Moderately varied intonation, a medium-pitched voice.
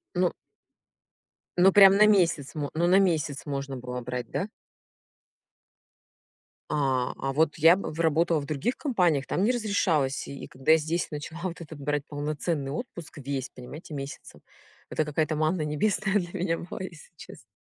Yes: average, 3.9 semitones; medium, 155 Hz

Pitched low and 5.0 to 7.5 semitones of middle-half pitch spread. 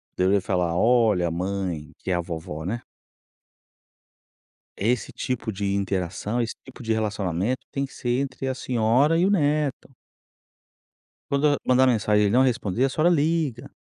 Yes: low, 115 Hz; wide, 5.5 semitones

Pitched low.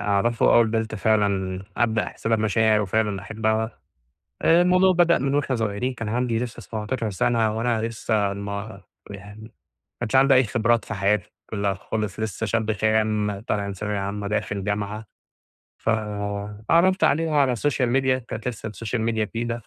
Yes: low, 110 Hz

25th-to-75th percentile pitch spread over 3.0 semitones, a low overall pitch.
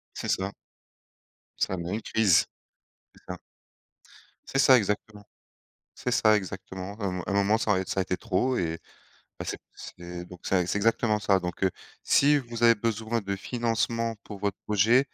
Yes: average, 3.4 semitones; low, 105 Hz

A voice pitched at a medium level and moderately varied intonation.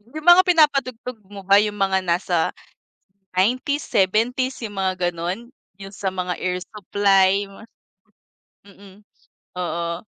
No: high, 195 Hz; average, 4.0 semitones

